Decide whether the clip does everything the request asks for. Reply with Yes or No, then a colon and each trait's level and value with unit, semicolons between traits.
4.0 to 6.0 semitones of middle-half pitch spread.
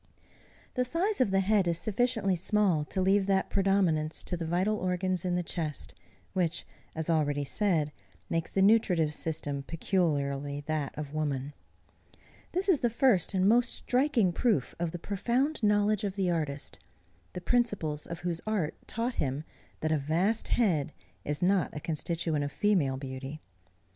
Yes: average, 5.2 semitones